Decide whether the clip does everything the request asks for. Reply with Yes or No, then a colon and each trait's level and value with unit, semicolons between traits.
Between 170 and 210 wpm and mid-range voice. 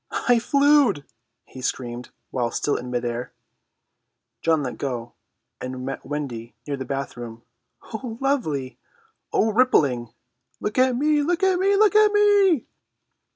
No: average, 140 wpm; medium, 150 Hz